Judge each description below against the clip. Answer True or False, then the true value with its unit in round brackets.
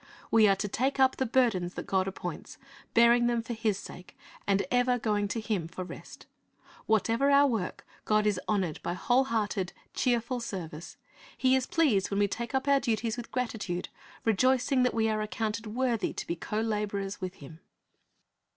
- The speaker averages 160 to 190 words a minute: True (180 wpm)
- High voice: True (220 Hz)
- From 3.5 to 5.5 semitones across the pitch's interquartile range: True (3.8 semitones)